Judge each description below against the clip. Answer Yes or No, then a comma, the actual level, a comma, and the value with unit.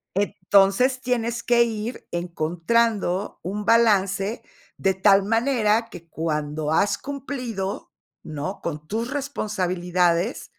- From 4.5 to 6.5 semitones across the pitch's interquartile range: Yes, average, 4.8 semitones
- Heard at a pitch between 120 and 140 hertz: No, high, 200 Hz